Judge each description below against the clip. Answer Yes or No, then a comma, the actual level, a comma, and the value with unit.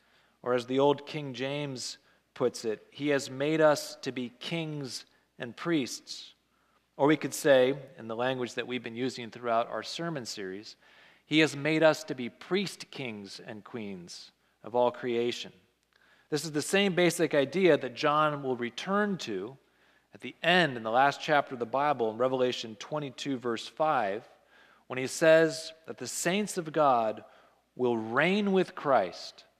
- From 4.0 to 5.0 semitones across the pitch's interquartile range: Yes, average, 4.3 semitones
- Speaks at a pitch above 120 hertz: Yes, medium, 140 Hz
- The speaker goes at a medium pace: Yes, average, 170 wpm